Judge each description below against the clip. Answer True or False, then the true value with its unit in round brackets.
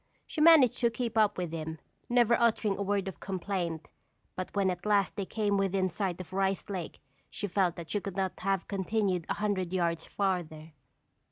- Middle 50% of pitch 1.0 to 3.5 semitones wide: True (2.5 semitones)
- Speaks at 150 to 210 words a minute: True (190 wpm)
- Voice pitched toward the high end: True (195 Hz)